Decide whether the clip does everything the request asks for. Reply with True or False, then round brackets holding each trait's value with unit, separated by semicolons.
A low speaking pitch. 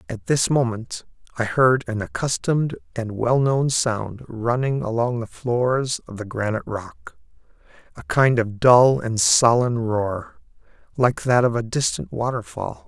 True (115 Hz)